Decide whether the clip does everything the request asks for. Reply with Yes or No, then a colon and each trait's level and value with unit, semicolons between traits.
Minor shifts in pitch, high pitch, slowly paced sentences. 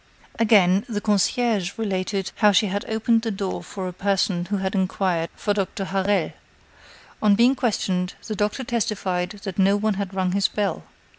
No: narrow, 2.1 semitones; high, 200 Hz; average, 170 wpm